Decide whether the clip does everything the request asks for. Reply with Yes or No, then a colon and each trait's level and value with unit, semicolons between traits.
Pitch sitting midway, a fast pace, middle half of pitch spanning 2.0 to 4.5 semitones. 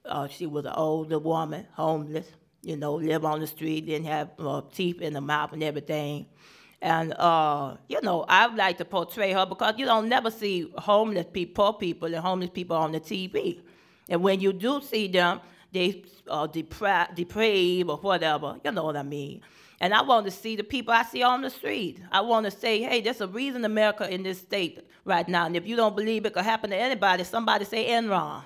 No: medium, 180 Hz; fast, 215 wpm; average, 5.0 semitones